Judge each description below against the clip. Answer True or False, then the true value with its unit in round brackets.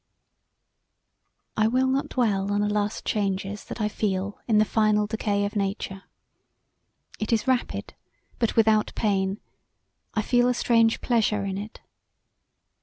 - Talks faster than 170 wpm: False (140 wpm)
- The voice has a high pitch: True (210 Hz)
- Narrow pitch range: True (1.9 semitones)